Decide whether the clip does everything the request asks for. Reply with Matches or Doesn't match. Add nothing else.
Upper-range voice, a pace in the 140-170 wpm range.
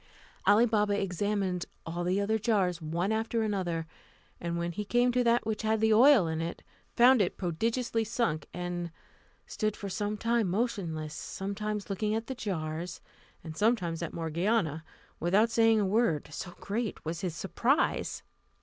Matches